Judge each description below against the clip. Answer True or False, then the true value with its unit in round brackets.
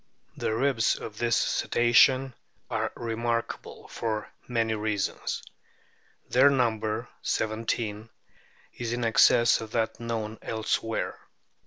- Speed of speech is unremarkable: False (105 wpm)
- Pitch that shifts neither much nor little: False (1.3 semitones)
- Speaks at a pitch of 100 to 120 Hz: True (115 Hz)